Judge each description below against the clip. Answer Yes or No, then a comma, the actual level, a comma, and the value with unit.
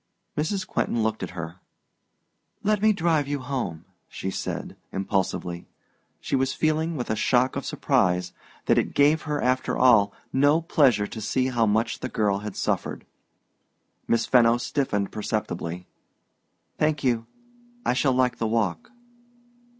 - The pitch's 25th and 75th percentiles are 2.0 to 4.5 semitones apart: No, wide, 5.6 semitones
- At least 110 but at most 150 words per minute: Yes, average, 145 wpm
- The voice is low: Yes, low, 120 Hz